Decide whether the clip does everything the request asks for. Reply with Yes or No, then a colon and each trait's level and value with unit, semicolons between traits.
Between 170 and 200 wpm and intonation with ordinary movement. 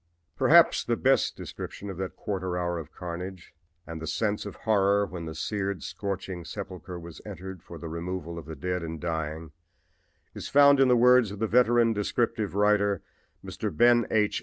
Yes: average, 180 wpm; average, 3.8 semitones